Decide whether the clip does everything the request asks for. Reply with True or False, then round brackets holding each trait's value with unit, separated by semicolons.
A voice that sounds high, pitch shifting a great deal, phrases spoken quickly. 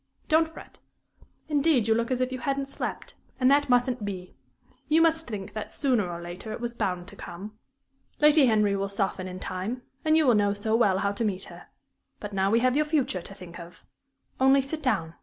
True (225 Hz; 5.8 semitones; 215 wpm)